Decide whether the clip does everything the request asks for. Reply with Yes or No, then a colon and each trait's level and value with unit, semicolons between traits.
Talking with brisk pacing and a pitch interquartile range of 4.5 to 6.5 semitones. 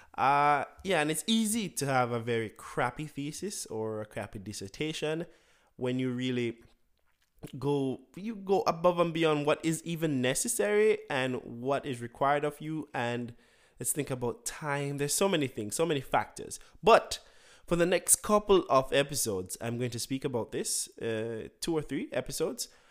No: average, 170 wpm; average, 5.2 semitones